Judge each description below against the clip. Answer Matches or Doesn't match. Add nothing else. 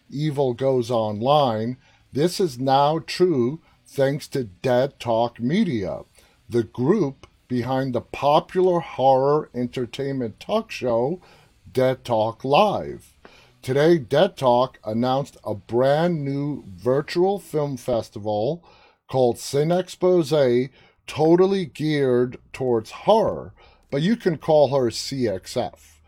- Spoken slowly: Matches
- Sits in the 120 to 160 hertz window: Matches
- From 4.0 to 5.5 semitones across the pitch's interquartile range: Matches